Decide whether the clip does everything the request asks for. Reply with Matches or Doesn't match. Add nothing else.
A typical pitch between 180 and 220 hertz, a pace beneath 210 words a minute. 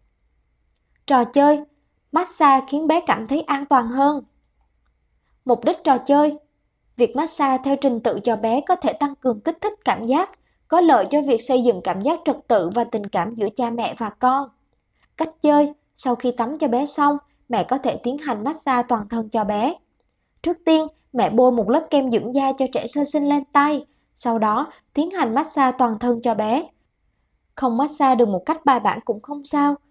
Doesn't match